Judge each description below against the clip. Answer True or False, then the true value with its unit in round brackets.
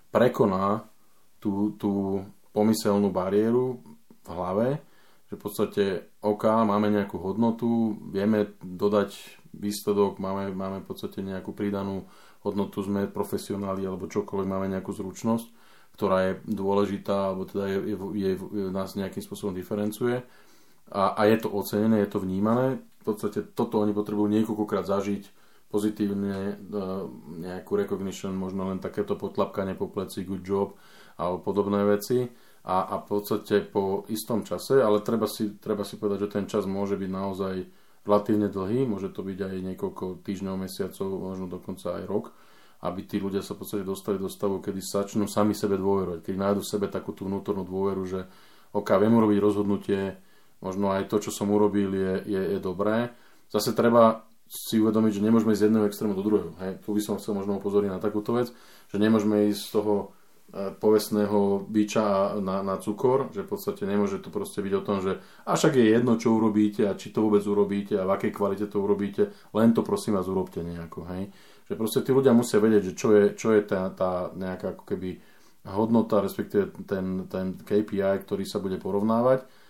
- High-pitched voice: False (100 Hz)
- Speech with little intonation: True (1.7 semitones)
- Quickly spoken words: True (175 wpm)